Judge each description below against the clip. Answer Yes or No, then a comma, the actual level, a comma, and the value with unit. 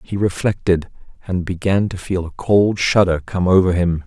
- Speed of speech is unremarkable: Yes, average, 175 wpm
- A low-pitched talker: Yes, very low, 90 Hz